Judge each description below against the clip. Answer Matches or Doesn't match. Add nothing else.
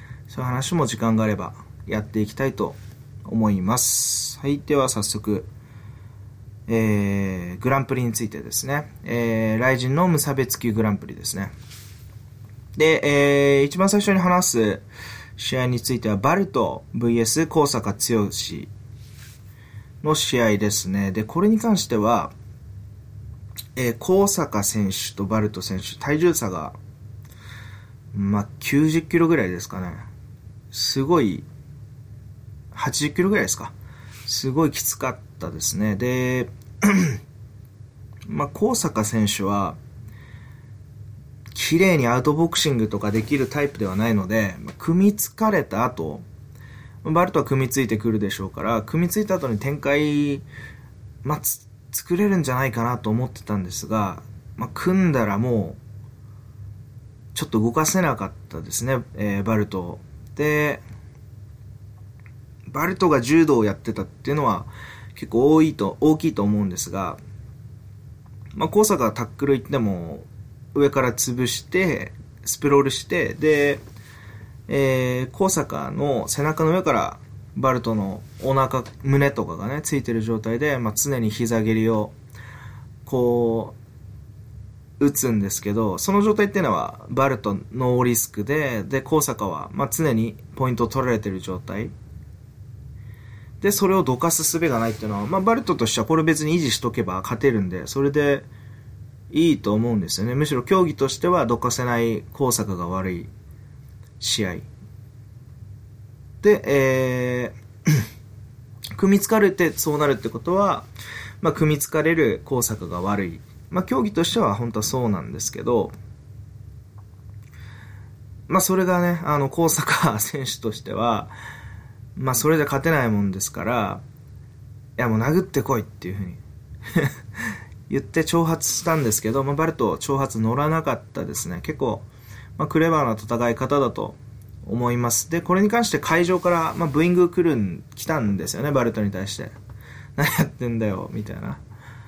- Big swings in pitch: Doesn't match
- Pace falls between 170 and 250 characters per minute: Doesn't match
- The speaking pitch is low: Matches